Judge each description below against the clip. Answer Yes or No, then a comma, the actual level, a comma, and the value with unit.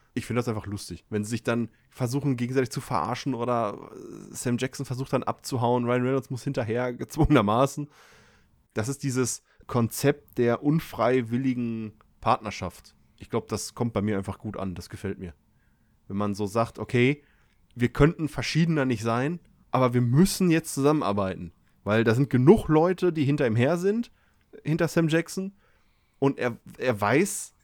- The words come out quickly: No, average, 165 wpm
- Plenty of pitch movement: No, average, 4.6 semitones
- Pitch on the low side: Yes, low, 125 Hz